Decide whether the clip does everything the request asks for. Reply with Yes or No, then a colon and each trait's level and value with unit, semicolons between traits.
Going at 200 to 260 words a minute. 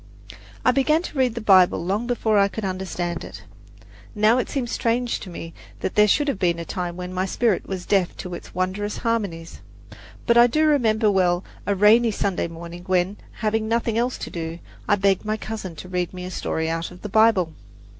Yes: fast, 205 wpm